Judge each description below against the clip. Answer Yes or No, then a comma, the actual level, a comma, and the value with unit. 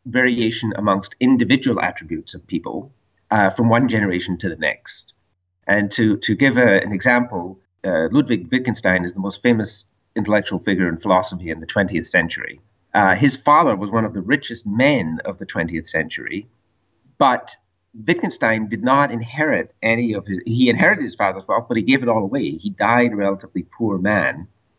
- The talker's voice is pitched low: Yes, low, 105 Hz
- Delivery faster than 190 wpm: No, average, 175 wpm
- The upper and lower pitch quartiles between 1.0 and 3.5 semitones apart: No, average, 3.9 semitones